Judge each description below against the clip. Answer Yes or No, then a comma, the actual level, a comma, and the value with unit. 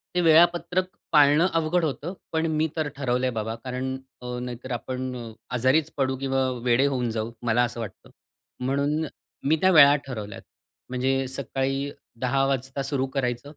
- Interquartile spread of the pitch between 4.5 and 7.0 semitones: No, average, 2.9 semitones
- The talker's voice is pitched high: No, low, 135 Hz